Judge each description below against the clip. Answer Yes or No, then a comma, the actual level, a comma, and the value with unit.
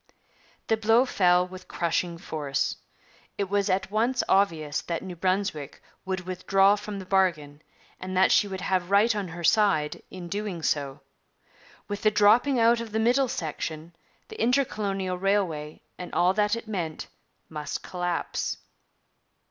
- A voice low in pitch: No, high, 190 Hz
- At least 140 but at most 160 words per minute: Yes, average, 150 wpm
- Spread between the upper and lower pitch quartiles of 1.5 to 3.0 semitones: No, average, 3.4 semitones